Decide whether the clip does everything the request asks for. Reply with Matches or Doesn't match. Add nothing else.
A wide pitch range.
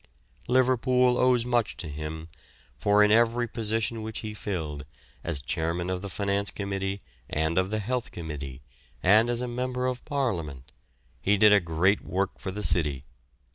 Matches